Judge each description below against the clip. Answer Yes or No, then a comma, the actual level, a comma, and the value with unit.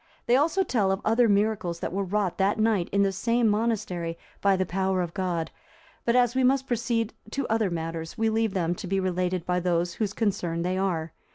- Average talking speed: No, fast, 210 wpm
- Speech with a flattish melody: No, average, 4.0 semitones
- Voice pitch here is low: No, high, 195 Hz